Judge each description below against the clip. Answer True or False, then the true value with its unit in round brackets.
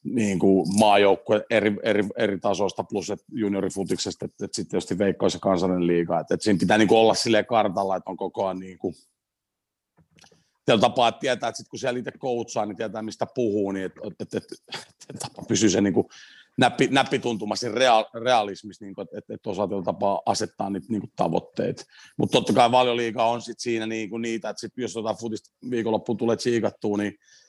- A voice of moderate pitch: False (110 Hz)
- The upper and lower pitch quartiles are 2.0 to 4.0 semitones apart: True (2.8 semitones)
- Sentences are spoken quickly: True (200 wpm)